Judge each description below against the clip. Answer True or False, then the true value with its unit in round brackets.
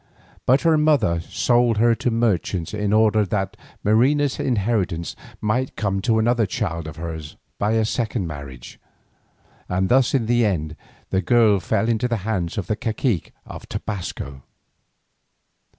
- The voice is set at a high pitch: False (105 Hz)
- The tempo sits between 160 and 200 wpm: False (150 wpm)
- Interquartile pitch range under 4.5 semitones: False (4.8 semitones)